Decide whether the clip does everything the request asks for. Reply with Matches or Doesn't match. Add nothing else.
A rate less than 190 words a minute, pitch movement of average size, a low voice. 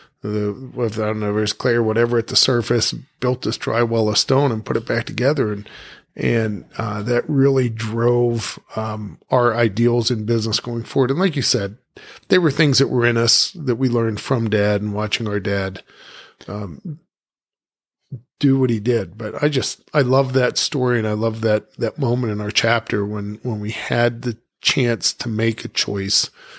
Doesn't match